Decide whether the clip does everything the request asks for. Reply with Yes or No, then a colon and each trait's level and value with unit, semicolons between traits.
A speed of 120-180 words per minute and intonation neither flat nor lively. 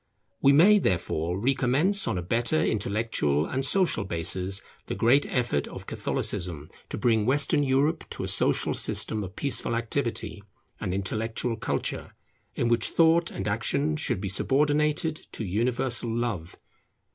No: average, 145 wpm; wide, 6.4 semitones